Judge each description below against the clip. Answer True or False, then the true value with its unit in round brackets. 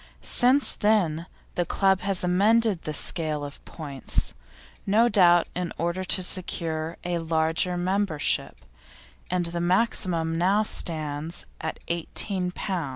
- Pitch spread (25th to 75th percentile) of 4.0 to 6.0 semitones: False (2.9 semitones)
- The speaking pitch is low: False (175 Hz)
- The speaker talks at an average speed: False (125 wpm)